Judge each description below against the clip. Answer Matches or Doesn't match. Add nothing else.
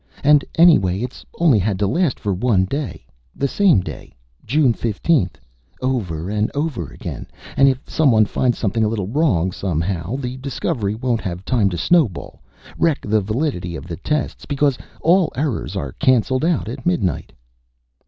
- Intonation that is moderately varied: Doesn't match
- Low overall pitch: Matches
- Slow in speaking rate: Doesn't match